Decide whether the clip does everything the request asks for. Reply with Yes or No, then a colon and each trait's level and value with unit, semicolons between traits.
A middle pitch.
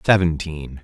No: very low, 80 Hz